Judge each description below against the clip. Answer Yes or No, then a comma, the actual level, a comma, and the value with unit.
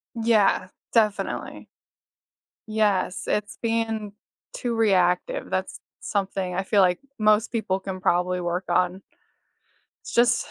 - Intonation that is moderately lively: Yes, average, 3.3 semitones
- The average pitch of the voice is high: Yes, high, 200 Hz